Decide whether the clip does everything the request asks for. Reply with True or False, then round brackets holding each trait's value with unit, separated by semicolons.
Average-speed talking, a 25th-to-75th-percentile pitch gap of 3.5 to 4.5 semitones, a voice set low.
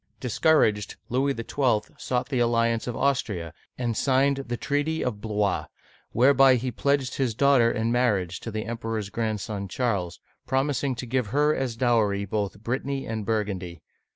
True (155 wpm; 3.8 semitones; 120 Hz)